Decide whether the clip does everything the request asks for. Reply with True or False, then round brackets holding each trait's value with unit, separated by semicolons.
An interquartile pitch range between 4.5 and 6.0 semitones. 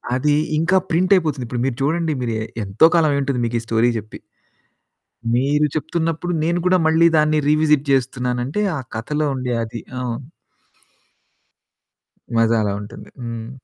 True (5.0 semitones)